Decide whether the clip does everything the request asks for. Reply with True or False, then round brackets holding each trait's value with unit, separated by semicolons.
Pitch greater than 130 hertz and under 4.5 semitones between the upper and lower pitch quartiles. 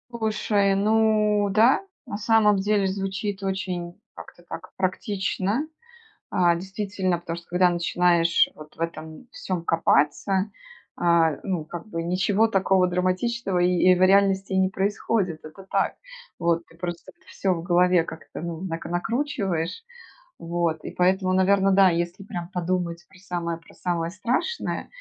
True (185 Hz; 2.6 semitones)